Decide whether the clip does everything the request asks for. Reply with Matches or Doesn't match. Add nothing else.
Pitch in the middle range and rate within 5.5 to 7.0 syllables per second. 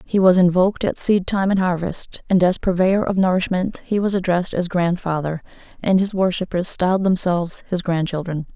Doesn't match